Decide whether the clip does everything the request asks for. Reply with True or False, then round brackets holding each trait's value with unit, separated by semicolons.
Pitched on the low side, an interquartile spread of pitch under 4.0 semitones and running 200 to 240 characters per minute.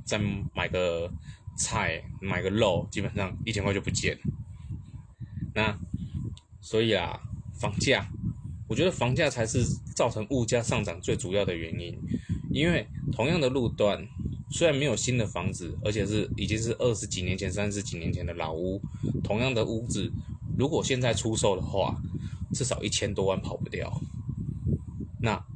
True (105 Hz; 3.6 semitones; 230 characters per minute)